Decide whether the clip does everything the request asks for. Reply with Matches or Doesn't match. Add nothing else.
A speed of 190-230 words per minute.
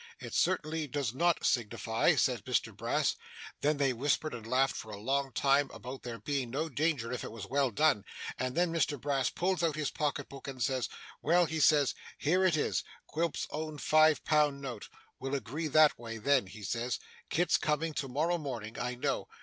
Matches